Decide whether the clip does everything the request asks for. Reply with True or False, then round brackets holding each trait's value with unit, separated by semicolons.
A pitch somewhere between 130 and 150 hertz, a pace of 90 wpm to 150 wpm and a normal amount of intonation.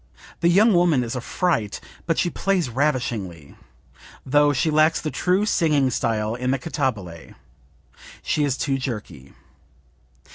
False (135 Hz; 140 wpm; 6.0 semitones)